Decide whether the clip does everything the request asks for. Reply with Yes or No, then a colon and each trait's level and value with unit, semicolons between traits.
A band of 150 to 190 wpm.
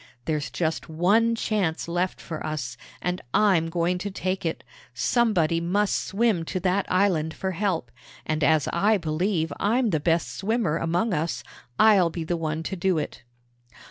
Yes: average, 165 wpm